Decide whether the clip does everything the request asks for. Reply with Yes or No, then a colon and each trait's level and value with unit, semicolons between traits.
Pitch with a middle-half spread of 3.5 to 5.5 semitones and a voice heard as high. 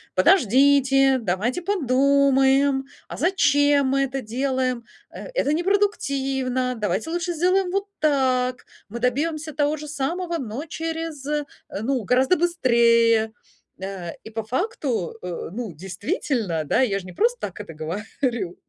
Yes: average, 5.0 semitones; very high, 265 Hz